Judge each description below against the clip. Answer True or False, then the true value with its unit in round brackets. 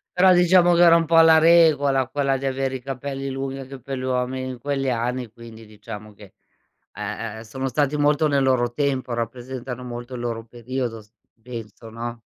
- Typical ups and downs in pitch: True (3.0 semitones)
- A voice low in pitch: True (130 Hz)